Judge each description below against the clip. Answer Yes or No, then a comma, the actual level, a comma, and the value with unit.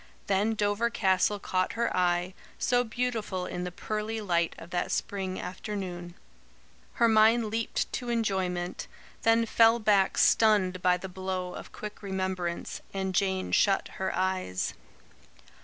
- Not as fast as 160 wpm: Yes, average, 140 wpm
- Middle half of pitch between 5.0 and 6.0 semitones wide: No, average, 3.0 semitones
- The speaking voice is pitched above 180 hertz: Yes, high, 190 Hz